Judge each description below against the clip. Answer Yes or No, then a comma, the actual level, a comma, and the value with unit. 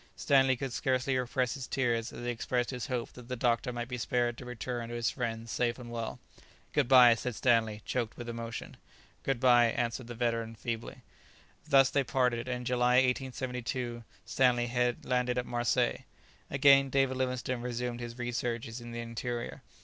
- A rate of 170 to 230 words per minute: Yes, average, 175 wpm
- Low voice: Yes, low, 120 Hz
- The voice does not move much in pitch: Yes, narrow, 1.3 semitones